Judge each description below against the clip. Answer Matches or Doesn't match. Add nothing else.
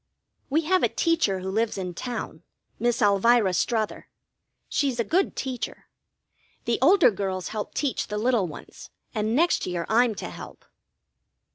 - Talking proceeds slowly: Doesn't match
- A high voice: Matches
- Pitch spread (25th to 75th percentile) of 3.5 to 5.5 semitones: Matches